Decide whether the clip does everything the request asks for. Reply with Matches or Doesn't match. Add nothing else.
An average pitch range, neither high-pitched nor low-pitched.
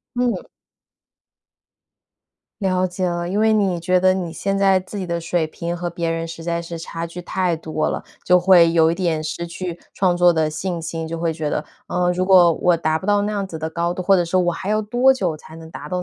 Doesn't match